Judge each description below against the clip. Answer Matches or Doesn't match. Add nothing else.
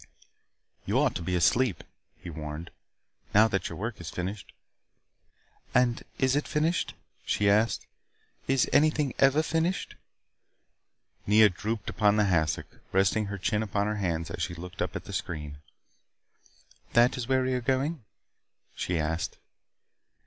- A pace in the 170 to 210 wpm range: Doesn't match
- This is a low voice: Matches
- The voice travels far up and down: Matches